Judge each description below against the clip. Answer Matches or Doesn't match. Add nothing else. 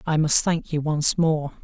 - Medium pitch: Matches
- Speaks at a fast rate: Matches